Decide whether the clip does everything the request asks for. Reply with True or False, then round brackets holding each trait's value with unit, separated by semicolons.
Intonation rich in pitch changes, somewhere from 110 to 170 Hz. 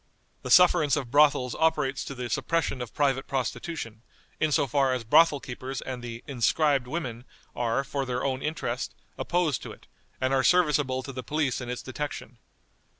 False (3.1 semitones; 135 Hz)